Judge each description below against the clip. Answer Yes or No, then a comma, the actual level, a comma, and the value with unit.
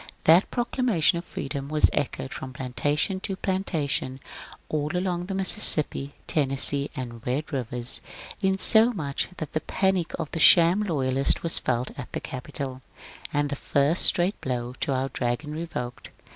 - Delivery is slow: No, average, 150 wpm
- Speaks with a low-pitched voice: No, medium, 145 Hz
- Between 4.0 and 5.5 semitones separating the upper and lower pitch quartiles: Yes, average, 5.1 semitones